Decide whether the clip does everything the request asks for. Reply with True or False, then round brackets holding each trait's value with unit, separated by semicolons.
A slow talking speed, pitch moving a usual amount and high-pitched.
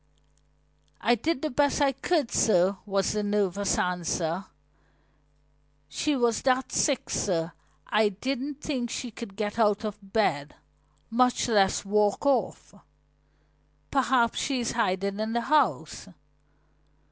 True (125 wpm; 4.6 semitones; 220 Hz)